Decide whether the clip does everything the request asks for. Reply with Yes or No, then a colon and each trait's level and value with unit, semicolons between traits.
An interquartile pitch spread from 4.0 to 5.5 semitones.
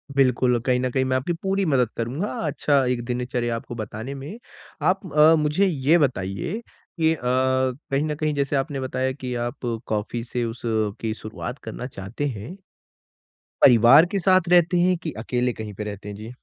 Yes: average, 4.4 semitones